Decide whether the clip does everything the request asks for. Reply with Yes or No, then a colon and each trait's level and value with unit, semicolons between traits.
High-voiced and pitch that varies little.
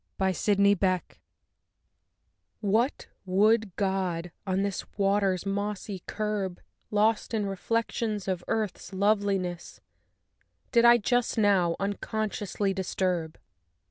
Yes: high, 200 Hz; narrow, 2.2 semitones